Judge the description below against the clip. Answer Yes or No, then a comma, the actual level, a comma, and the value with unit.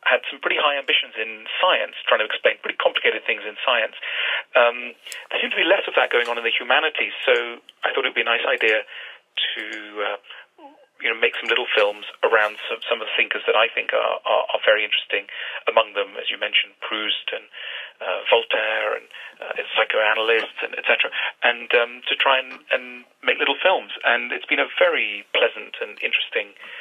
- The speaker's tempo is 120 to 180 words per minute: No, average, 200 wpm